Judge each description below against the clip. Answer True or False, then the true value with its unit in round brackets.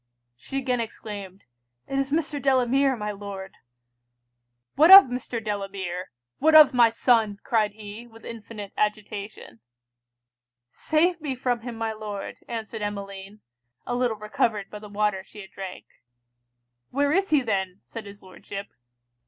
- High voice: True (220 Hz)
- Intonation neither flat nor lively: True (3.9 semitones)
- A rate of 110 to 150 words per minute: True (145 wpm)